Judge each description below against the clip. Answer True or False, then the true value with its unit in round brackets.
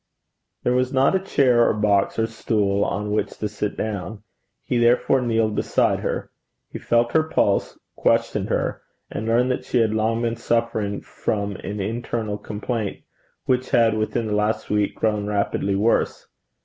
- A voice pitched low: True (110 Hz)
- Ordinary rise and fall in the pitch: False (2.3 semitones)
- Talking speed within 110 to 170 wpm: True (165 wpm)